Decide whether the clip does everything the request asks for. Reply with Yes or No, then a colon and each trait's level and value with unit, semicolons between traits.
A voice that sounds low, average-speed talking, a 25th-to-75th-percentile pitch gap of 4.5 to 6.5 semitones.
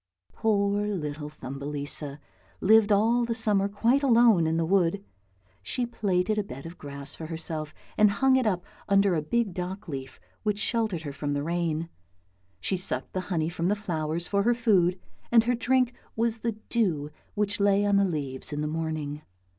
No: high, 190 Hz; average, 180 wpm; wide, 5.4 semitones